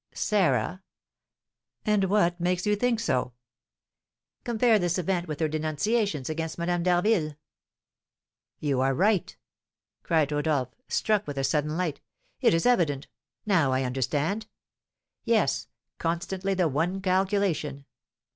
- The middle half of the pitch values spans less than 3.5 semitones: No, average, 4.9 semitones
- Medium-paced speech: No, slow, 120 wpm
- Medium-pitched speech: Yes, medium, 170 Hz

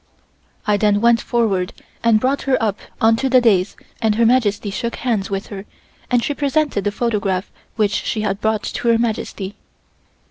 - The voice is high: Yes, high, 220 Hz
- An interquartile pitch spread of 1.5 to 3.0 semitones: Yes, average, 2.7 semitones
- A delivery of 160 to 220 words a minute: Yes, average, 175 wpm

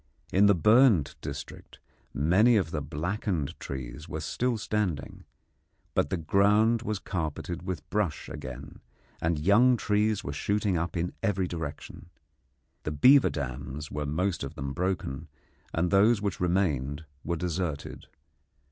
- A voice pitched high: No, very low, 90 Hz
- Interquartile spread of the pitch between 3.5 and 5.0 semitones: No, wide, 5.5 semitones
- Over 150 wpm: No, average, 140 wpm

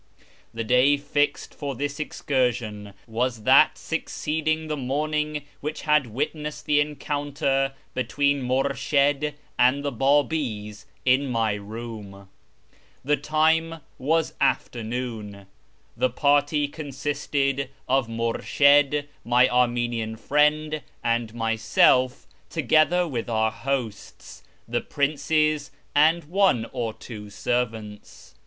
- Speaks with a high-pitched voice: No, low, 135 Hz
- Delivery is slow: Yes, slow, 105 wpm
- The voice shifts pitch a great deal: No, average, 4.2 semitones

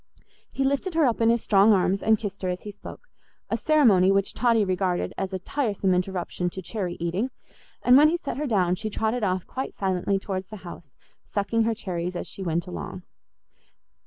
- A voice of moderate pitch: No, high, 195 Hz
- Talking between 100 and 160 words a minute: No, average, 200 wpm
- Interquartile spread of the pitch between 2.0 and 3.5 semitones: No, average, 4.0 semitones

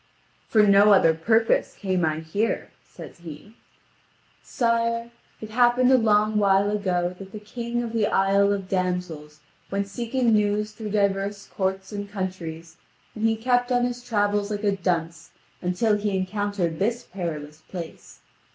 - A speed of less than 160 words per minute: Yes, average, 150 wpm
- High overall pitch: Yes, high, 205 Hz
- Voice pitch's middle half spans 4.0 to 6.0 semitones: No, average, 3.2 semitones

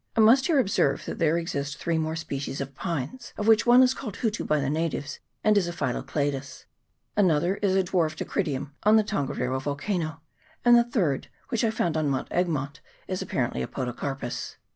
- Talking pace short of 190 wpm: No, average, 195 wpm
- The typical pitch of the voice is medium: Yes, medium, 165 Hz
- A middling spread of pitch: No, wide, 6.9 semitones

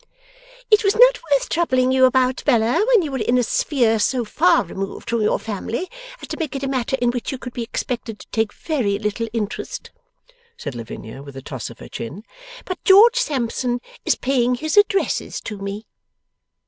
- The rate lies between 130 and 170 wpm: No, average, 195 wpm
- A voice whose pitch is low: No, very high, 250 Hz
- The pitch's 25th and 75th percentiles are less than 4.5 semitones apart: No, wide, 5.5 semitones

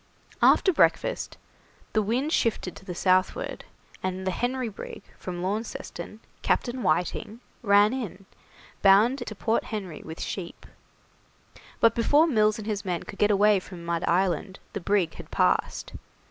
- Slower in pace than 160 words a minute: Yes, average, 145 wpm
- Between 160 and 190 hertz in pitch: No, high, 205 Hz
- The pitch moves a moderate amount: Yes, average, 3.5 semitones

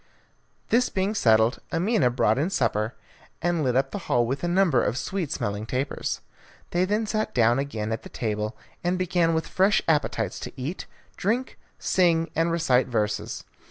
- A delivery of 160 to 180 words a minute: Yes, average, 170 wpm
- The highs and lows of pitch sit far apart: Yes, wide, 7.5 semitones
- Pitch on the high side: No, medium, 150 Hz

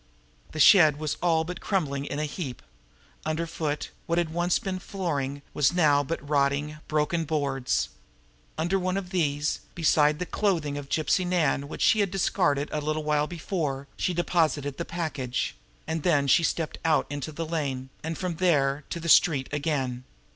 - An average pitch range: Yes, average, 3.2 semitones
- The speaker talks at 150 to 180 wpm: Yes, average, 170 wpm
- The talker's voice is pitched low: No, medium, 155 Hz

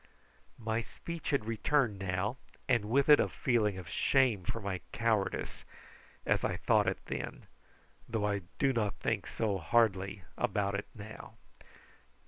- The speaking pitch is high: No, low, 110 Hz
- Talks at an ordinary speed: Yes, average, 145 wpm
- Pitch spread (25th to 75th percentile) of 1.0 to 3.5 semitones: Yes, average, 3.1 semitones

